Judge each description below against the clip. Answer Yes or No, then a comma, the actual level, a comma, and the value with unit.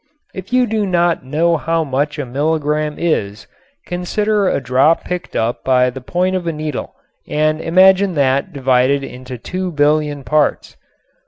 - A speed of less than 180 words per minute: Yes, average, 155 wpm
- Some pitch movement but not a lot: Yes, average, 4.7 semitones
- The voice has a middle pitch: Yes, medium, 155 Hz